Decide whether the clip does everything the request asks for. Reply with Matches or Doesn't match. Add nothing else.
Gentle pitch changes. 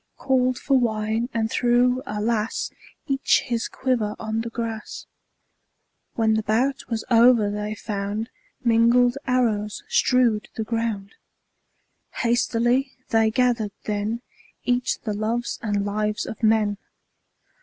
Matches